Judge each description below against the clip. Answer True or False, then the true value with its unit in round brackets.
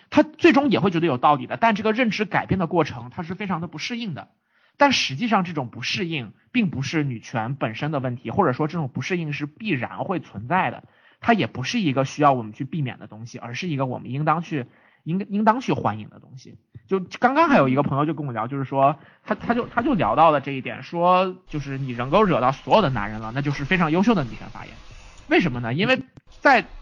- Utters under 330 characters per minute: False (355 characters per minute)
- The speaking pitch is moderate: True (150 Hz)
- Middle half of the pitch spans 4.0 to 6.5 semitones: False (6.9 semitones)